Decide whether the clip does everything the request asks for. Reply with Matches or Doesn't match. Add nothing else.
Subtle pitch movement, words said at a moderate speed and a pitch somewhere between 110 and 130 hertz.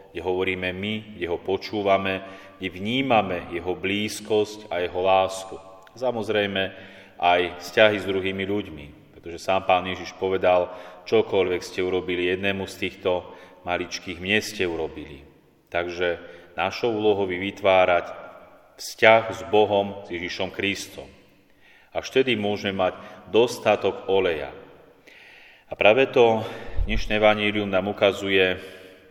Doesn't match